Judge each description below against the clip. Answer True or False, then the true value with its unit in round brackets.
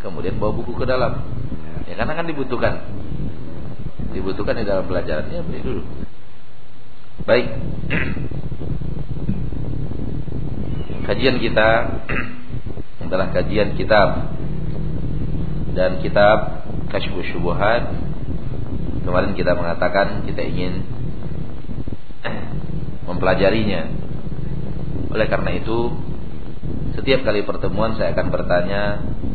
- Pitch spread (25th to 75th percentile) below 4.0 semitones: False (4.6 semitones)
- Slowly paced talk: True (80 wpm)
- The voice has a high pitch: False (100 Hz)